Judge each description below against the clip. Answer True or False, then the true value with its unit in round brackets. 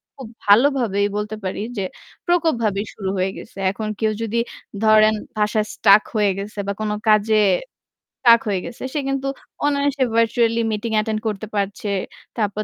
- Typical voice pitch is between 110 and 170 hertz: False (215 Hz)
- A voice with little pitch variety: True (2.2 semitones)